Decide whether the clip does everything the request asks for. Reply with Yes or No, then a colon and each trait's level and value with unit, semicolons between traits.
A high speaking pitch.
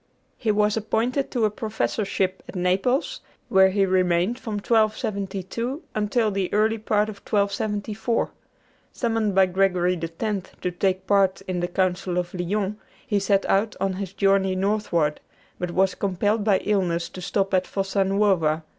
Yes: high, 195 Hz